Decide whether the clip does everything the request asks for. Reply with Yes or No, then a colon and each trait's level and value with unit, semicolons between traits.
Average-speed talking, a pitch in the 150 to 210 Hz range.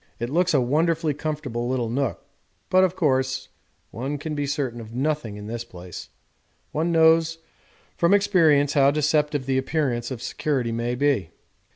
No: average, 160 wpm; medium, 140 Hz